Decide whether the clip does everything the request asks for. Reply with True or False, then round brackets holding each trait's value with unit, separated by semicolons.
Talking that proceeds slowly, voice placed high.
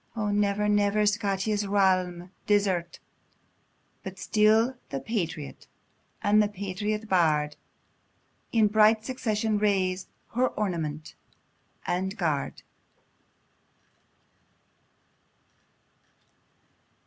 True (75 wpm; 205 Hz)